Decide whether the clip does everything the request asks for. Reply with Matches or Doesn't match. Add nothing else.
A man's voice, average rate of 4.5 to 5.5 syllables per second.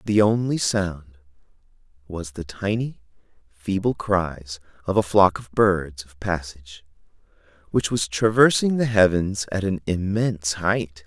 Doesn't match